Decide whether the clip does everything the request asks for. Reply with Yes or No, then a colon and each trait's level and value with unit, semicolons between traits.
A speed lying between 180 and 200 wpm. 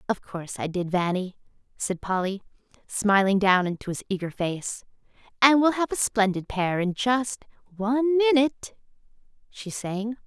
No: slow, 135 wpm